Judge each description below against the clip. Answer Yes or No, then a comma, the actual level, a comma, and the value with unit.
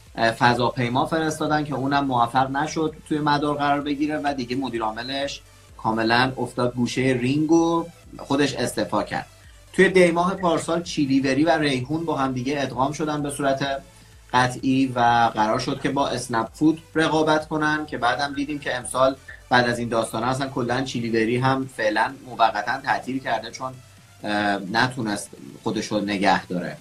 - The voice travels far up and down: No, average, 3.9 semitones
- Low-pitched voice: Yes, low, 130 Hz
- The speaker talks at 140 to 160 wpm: Yes, average, 150 wpm